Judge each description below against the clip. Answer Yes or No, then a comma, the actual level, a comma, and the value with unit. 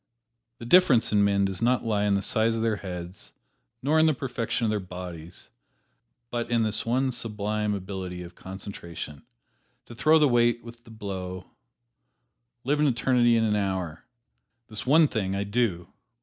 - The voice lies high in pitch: No, low, 105 Hz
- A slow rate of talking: No, average, 170 wpm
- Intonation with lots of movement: No, average, 3.9 semitones